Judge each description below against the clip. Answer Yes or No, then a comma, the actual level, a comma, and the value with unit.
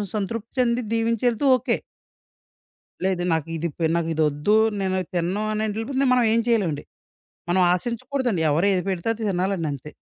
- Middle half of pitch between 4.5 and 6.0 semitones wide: Yes, average, 5.2 semitones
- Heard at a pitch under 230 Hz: Yes, high, 200 Hz